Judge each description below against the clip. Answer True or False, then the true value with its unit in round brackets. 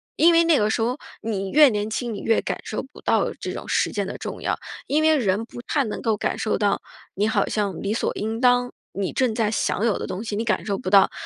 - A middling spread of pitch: True (3.1 semitones)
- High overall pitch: True (220 Hz)